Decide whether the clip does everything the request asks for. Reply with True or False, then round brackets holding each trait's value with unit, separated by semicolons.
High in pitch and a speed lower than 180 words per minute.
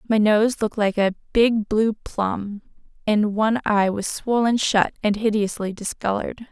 True (215 Hz; 155 wpm)